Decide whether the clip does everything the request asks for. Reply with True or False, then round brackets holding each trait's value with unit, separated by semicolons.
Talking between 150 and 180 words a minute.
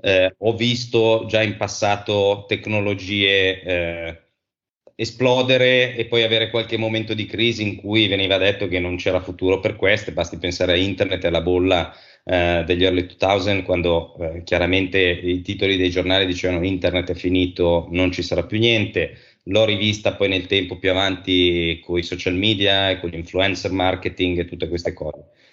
True (170 wpm)